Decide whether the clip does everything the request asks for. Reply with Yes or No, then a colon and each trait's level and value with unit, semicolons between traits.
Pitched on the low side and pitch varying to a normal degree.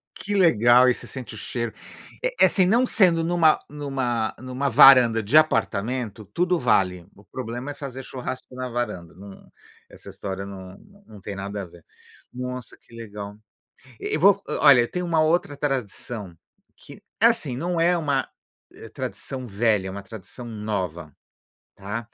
No: low, 120 Hz; wide, 5.9 semitones